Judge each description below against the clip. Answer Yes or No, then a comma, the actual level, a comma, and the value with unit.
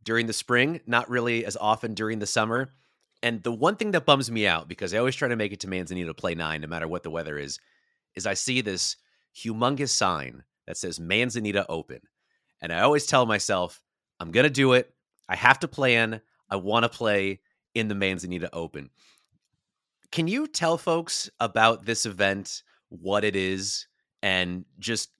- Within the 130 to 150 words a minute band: No, average, 190 wpm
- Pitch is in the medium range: No, low, 110 Hz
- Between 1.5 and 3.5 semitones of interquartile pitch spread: No, average, 4.5 semitones